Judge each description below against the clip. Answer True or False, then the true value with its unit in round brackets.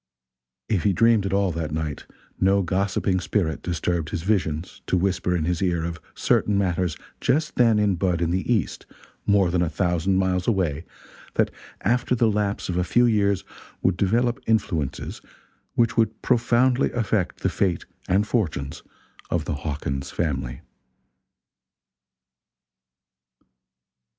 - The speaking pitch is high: False (95 Hz)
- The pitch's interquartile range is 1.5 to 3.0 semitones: False (3.8 semitones)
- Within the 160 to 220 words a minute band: False (140 wpm)